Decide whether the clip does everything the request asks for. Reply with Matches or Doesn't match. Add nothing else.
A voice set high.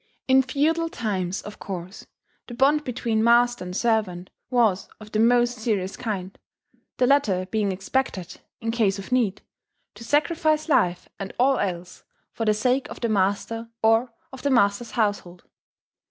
Matches